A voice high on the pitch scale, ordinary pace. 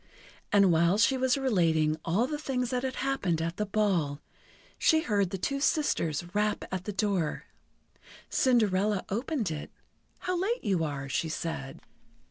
Yes: high, 200 Hz; average, 155 wpm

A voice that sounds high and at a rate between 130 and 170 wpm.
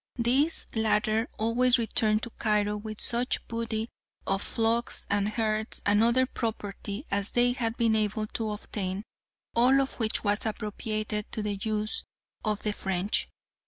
Yes: high, 220 Hz; average, 150 wpm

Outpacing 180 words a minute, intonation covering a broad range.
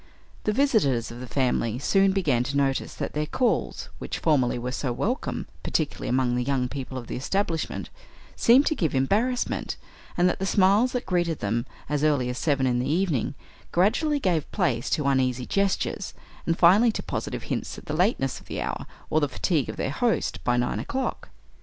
Yes: average, 190 wpm; wide, 7.4 semitones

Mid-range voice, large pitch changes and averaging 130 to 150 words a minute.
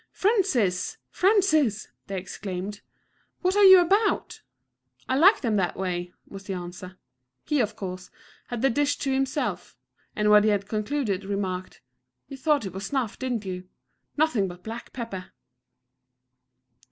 No: high, 215 Hz; wide, 7.1 semitones; average, 145 wpm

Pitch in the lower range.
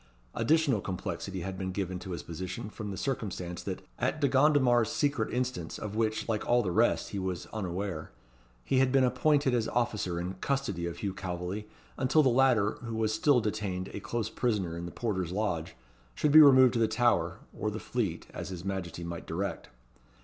Yes: low, 105 Hz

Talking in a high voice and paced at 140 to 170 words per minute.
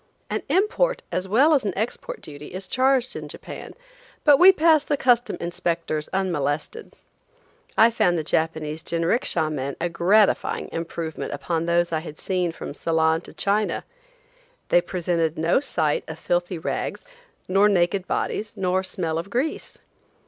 No: medium, 180 Hz; average, 150 wpm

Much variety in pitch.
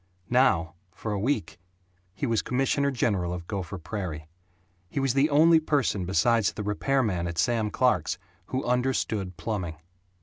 Yes: wide, 6.5 semitones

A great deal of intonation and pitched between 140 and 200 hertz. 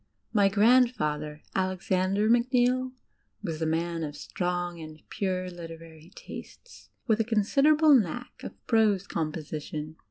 Yes: wide, 6.3 semitones; medium, 185 Hz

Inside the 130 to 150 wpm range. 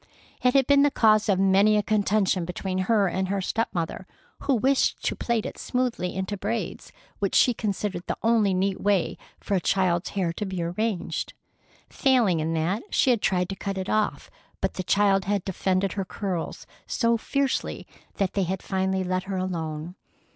No: average, 185 wpm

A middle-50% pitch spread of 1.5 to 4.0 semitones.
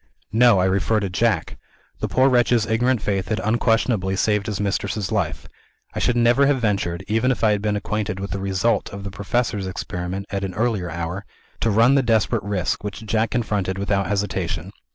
Yes: average, 2.9 semitones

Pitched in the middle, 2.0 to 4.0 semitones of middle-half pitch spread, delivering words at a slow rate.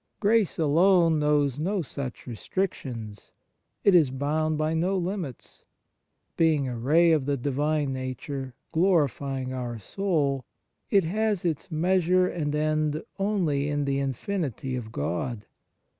No: medium, 150 Hz; average, 4.6 semitones; slow, 130 wpm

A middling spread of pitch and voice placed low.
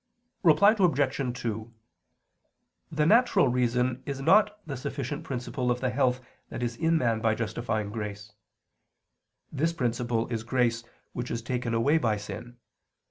Yes: average, 3.7 semitones; low, 125 Hz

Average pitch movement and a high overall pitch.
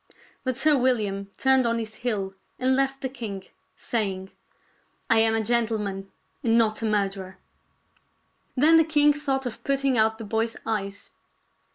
Yes: average, 4.3 semitones; high, 225 Hz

